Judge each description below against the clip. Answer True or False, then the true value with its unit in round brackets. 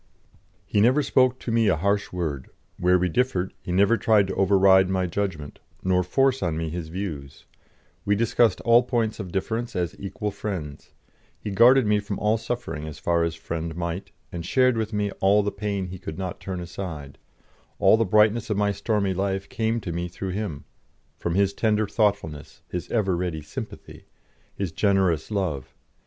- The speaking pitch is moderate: False (95 Hz)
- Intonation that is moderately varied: True (3.6 semitones)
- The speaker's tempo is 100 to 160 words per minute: False (180 wpm)